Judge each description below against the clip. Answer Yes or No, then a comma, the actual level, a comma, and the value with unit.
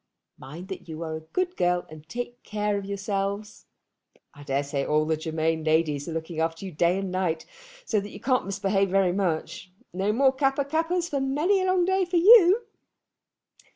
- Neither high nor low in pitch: No, high, 195 Hz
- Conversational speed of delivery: Yes, average, 190 wpm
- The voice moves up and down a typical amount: No, wide, 8.9 semitones